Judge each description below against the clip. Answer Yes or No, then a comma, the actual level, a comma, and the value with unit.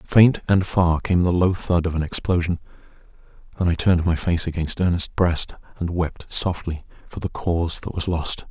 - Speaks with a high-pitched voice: No, very low, 85 Hz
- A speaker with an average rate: Yes, average, 190 wpm